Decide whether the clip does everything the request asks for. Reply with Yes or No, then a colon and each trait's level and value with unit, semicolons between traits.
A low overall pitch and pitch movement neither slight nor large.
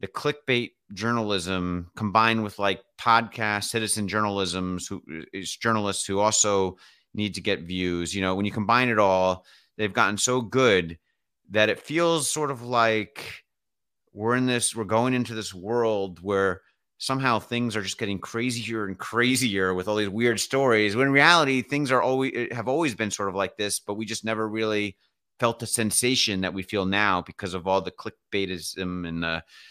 Yes: low, 105 Hz; average, 3.6 semitones